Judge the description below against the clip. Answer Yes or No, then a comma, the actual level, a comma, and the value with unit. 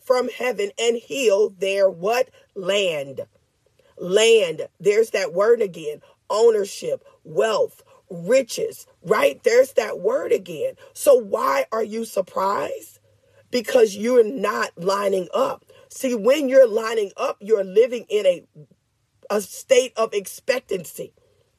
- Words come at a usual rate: No, slow, 120 wpm